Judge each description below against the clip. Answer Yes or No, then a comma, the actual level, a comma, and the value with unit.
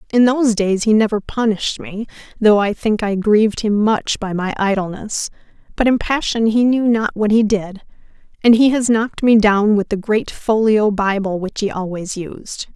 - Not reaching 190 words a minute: No, average, 195 wpm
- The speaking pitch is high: Yes, high, 215 Hz